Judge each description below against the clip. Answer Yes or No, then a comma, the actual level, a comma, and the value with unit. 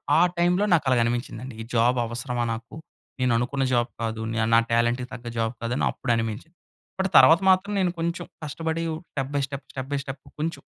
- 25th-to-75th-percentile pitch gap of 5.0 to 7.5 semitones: Yes, wide, 5.4 semitones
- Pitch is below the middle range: Yes, low, 130 Hz